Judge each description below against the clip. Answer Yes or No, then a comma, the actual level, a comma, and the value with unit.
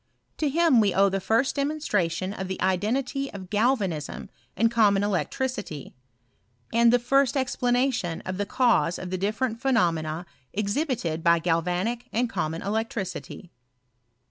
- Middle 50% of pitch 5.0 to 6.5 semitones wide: Yes, average, 5.3 semitones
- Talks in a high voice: Yes, high, 210 Hz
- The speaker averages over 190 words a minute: No, average, 145 wpm